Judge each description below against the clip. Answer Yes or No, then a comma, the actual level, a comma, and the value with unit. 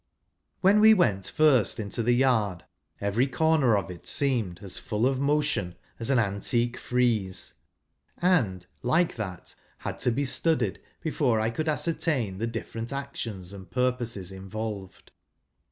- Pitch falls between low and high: No, low, 120 Hz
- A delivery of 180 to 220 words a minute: No, average, 140 wpm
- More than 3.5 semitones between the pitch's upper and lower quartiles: Yes, wide, 5.6 semitones